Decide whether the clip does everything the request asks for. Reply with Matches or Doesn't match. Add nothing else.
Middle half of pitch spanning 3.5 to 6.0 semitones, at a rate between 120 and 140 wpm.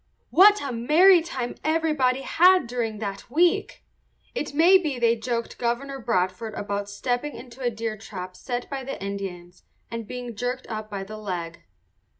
Doesn't match